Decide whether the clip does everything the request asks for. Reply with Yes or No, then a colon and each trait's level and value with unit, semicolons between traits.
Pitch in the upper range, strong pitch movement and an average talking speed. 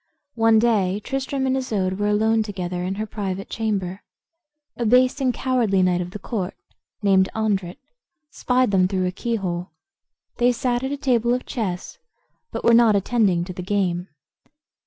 No: high, 210 Hz; average, 4.4 semitones; average, 165 wpm